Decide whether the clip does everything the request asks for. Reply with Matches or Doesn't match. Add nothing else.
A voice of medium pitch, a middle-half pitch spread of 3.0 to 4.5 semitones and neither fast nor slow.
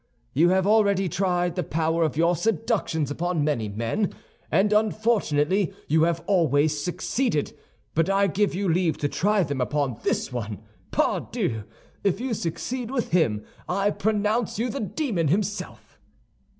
Doesn't match